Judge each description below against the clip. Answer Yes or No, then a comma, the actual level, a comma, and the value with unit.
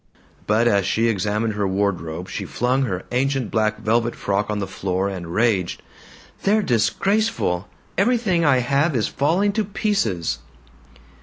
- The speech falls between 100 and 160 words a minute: Yes, average, 145 wpm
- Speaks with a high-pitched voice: No, low, 115 Hz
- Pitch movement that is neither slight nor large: No, wide, 6.8 semitones